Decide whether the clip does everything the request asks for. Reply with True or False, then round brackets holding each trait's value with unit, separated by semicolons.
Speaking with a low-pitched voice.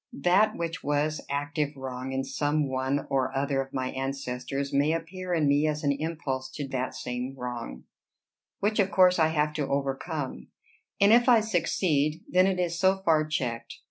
False (145 Hz)